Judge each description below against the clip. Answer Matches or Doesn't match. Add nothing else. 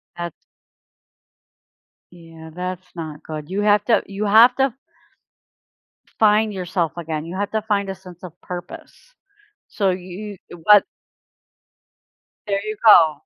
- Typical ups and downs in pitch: Matches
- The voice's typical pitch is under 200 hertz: Matches